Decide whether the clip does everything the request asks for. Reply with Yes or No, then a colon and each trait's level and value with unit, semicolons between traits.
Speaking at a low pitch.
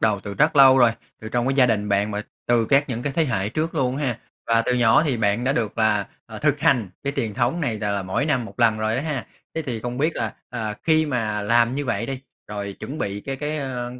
Yes: low, 120 Hz